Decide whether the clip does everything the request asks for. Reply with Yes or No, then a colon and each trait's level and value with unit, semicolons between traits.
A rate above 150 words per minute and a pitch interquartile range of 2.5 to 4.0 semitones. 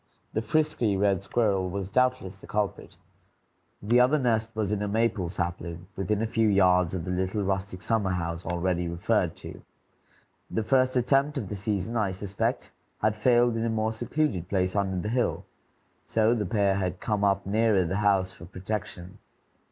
Yes: average, 175 wpm; average, 3.3 semitones